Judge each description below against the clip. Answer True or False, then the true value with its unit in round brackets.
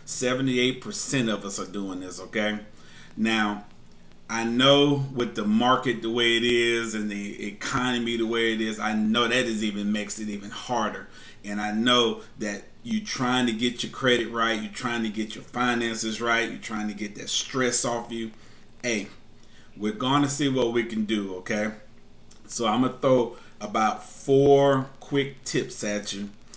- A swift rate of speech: False (175 wpm)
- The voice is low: True (115 Hz)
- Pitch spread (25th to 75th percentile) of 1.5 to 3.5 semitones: True (2.9 semitones)